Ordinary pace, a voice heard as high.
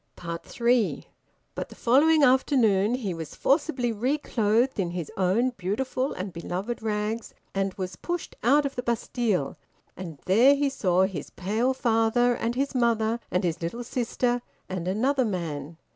Yes: average, 150 wpm; high, 225 Hz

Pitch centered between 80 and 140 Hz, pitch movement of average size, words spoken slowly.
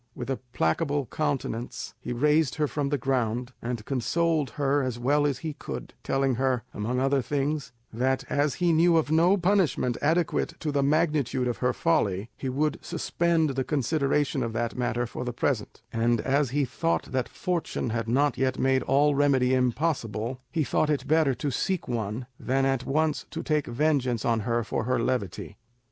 No: low, 135 Hz; average, 3.5 semitones; average, 185 wpm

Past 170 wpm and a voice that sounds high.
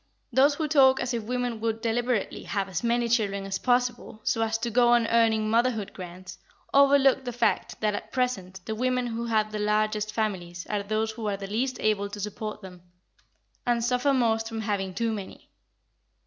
Yes: average, 190 wpm; high, 225 Hz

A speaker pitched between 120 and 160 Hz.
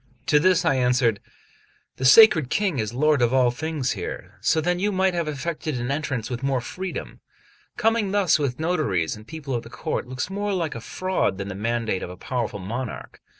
Yes: low, 135 Hz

